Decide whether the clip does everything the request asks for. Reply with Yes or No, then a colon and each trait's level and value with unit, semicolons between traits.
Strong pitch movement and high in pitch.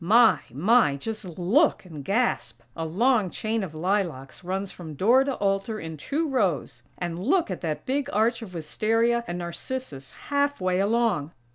Yes: wide, 5.7 semitones; high, 195 Hz